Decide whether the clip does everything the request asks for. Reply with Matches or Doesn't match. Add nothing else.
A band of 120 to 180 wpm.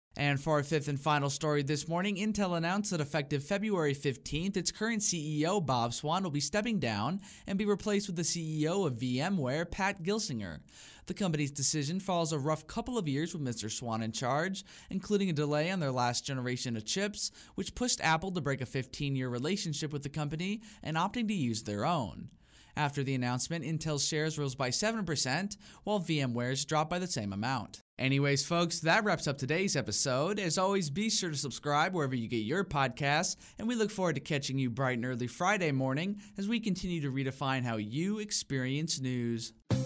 Doesn't match